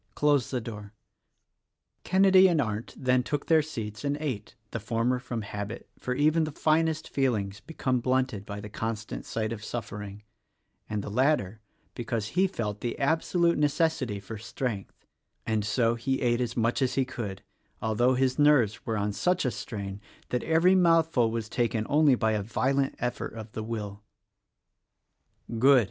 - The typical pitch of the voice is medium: No, low, 120 Hz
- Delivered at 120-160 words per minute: No, average, 170 wpm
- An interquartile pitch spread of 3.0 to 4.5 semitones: No, average, 5.0 semitones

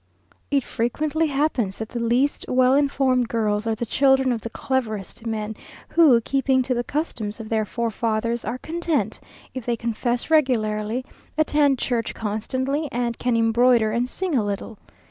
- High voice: Yes, high, 240 Hz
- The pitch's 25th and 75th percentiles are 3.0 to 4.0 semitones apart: Yes, average, 3.3 semitones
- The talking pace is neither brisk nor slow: Yes, average, 160 wpm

